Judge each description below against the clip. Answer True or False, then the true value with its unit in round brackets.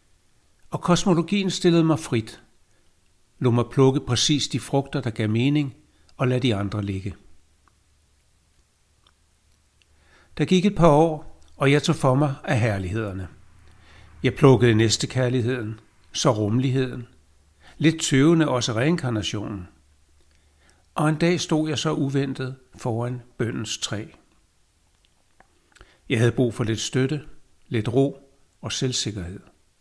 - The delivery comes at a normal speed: False (125 wpm)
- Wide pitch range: True (7.3 semitones)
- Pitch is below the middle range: True (120 Hz)